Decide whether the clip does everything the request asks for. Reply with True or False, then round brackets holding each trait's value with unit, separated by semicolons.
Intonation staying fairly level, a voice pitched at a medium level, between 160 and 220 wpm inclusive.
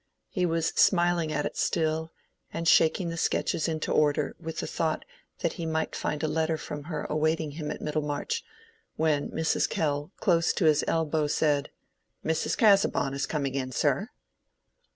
True (1.8 semitones; 155 Hz; 165 wpm)